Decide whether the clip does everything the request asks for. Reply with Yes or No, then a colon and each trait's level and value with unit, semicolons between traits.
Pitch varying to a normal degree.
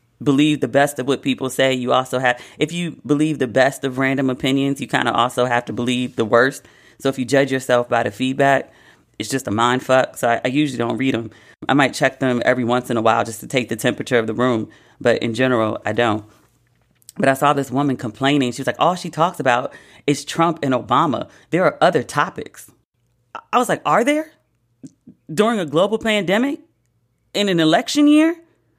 Yes: average, 3.2 semitones